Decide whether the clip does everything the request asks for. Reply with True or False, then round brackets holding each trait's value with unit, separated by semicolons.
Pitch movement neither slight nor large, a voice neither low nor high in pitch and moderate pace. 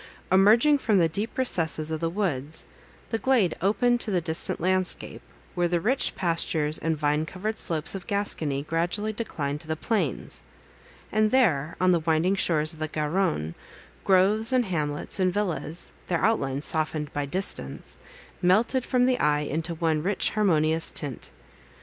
True (4.8 semitones; 175 Hz; 155 wpm)